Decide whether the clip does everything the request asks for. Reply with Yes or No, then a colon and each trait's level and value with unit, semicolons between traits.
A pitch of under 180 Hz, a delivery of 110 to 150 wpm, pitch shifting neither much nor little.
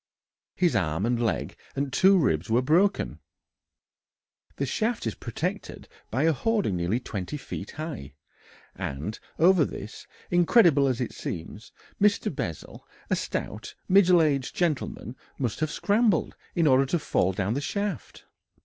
No: medium, 140 Hz; average, 140 wpm; wide, 8.2 semitones